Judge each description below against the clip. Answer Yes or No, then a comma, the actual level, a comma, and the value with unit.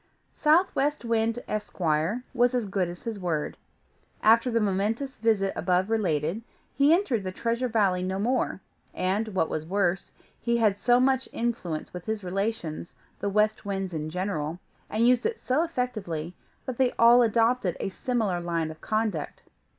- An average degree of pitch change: Yes, average, 4.7 semitones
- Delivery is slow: No, average, 160 wpm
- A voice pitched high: Yes, high, 215 Hz